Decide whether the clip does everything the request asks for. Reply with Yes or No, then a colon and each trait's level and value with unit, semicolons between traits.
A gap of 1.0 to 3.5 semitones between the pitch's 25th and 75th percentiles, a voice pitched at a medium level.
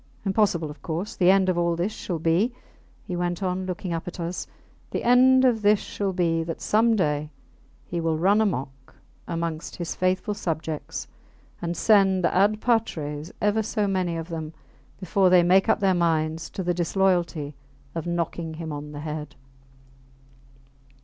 Yes: average, 3.1 semitones; medium, 175 Hz